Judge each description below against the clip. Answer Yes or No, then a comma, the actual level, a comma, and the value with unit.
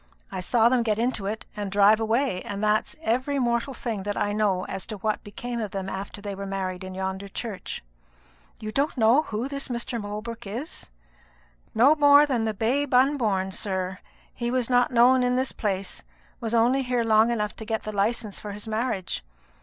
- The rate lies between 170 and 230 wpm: Yes, average, 195 wpm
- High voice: Yes, high, 220 Hz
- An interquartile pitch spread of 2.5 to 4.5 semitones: Yes, average, 3.5 semitones